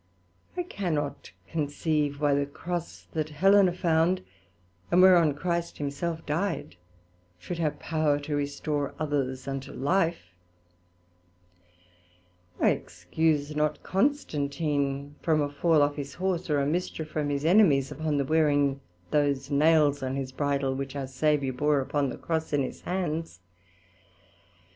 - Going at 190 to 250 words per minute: No, slow, 135 wpm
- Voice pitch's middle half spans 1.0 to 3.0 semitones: Yes, narrow, 2.6 semitones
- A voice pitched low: No, medium, 150 Hz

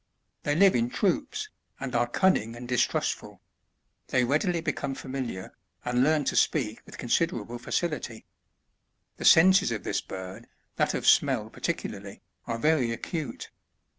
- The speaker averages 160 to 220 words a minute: No, slow, 135 wpm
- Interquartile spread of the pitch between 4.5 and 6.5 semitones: Yes, wide, 5.5 semitones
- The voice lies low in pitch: Yes, low, 130 Hz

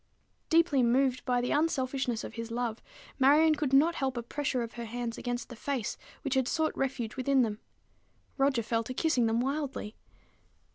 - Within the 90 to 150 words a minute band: No, average, 180 wpm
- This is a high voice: Yes, very high, 255 Hz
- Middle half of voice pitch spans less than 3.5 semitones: Yes, average, 2.9 semitones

